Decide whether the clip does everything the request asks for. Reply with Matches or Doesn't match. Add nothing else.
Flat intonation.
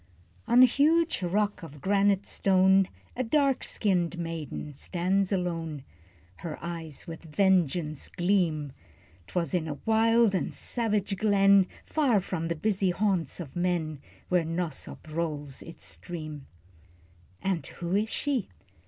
Doesn't match